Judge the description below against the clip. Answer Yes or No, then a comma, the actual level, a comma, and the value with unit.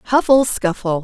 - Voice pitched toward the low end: No, high, 215 Hz